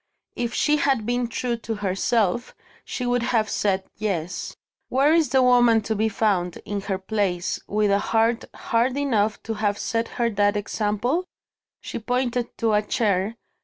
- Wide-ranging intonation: No, average, 3.1 semitones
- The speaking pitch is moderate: No, high, 225 Hz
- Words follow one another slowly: No, average, 165 wpm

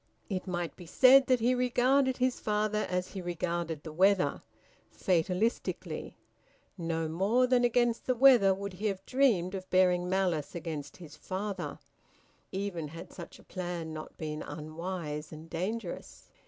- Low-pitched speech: No, medium, 185 Hz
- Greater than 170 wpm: No, average, 150 wpm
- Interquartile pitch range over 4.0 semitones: Yes, average, 4.8 semitones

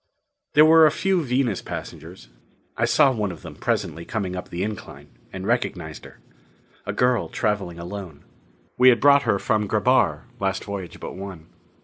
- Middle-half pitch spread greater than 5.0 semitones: Yes, wide, 5.6 semitones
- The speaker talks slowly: No, average, 165 wpm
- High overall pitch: No, low, 100 Hz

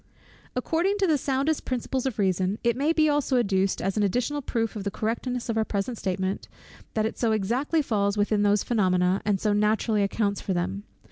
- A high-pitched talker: Yes, high, 220 Hz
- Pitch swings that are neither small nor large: Yes, average, 4.3 semitones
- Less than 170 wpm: No, fast, 205 wpm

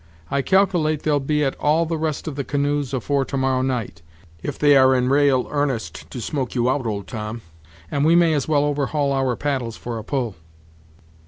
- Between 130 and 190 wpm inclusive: No, average, 200 wpm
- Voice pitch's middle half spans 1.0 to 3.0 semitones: Yes, narrow, 2.6 semitones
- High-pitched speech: No, medium, 140 Hz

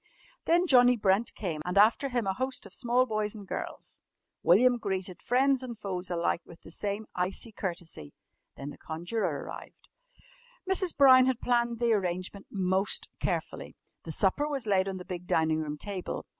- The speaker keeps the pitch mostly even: No, average, 5.3 semitones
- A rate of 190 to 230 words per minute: No, average, 170 wpm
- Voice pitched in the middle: No, high, 205 Hz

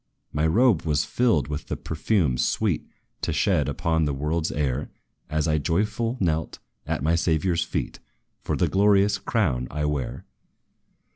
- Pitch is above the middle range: No, very low, 80 Hz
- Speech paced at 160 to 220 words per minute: No, average, 150 wpm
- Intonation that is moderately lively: Yes, average, 4.6 semitones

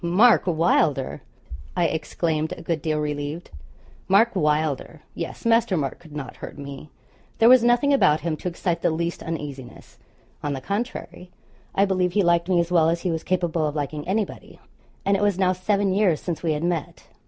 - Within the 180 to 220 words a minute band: Yes, average, 190 wpm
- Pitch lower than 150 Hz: No, medium, 170 Hz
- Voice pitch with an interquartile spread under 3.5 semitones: No, average, 3.8 semitones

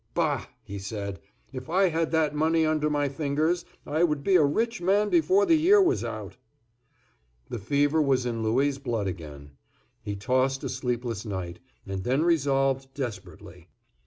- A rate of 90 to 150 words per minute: No, average, 160 wpm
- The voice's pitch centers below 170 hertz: Yes, medium, 140 Hz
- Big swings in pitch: Yes, wide, 6.3 semitones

